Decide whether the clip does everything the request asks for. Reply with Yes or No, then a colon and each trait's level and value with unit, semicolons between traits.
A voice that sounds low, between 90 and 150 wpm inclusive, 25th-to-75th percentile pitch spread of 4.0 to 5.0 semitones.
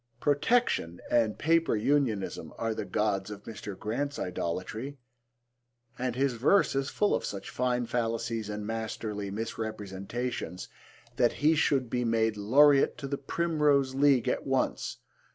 Yes: low, 120 Hz; slow, 135 wpm; average, 4.7 semitones